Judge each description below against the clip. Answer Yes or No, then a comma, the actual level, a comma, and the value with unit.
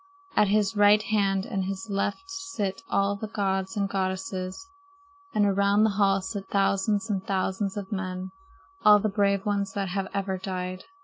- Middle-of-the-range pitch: No, high, 200 Hz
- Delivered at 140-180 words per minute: Yes, average, 170 wpm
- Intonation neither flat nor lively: No, narrow, 1.3 semitones